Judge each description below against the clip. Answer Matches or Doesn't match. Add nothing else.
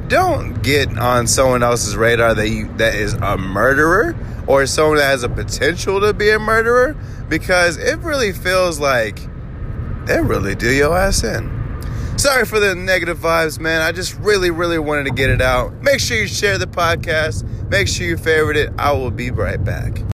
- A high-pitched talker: Doesn't match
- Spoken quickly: Doesn't match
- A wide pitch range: Matches